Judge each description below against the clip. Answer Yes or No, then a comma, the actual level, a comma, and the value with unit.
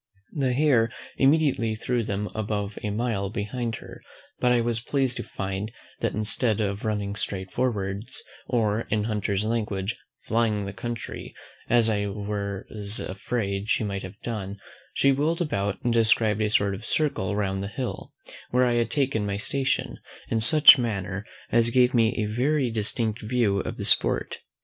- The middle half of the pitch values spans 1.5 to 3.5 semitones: Yes, average, 3.1 semitones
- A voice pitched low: Yes, low, 110 Hz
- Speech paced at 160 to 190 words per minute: Yes, average, 165 wpm